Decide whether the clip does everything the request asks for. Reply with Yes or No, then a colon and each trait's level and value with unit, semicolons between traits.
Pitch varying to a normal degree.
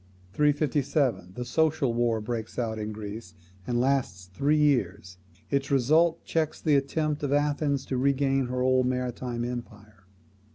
Yes: average, 4.3 semitones